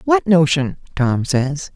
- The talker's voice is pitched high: No, medium, 160 Hz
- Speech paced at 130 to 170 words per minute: Yes, slow, 135 wpm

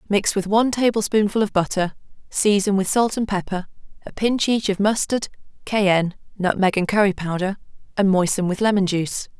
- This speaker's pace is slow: No, average, 165 wpm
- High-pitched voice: Yes, high, 200 Hz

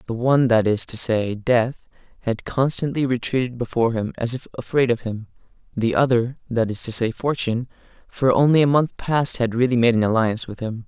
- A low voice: Yes, low, 120 Hz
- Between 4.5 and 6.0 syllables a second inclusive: Yes, 5.5 syllables/s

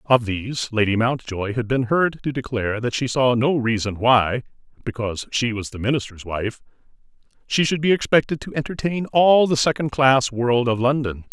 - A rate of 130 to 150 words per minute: No, average, 180 wpm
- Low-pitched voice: Yes, low, 125 Hz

